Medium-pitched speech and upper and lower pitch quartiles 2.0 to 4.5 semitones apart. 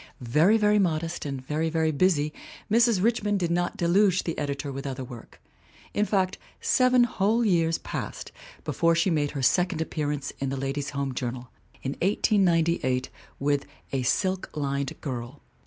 No: medium, 160 Hz; average, 5.3 semitones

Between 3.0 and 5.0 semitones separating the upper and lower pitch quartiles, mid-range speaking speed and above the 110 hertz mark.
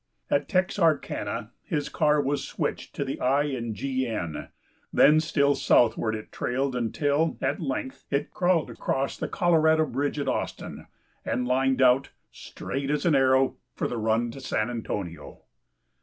Yes: average, 3.5 semitones; average, 155 wpm; low, 135 Hz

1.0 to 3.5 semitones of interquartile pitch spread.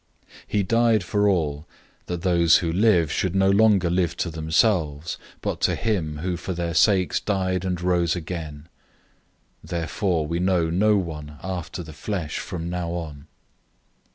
Yes: average, 2.7 semitones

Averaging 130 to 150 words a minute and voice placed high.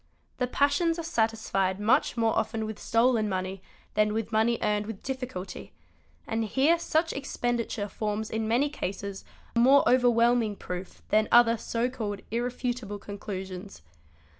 Yes: average, 140 wpm; high, 225 Hz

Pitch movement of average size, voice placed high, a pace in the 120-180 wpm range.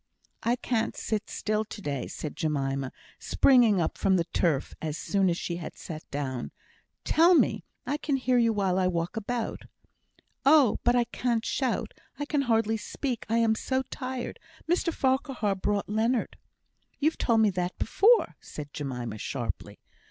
No: wide, 6.8 semitones; high, 220 Hz; average, 165 wpm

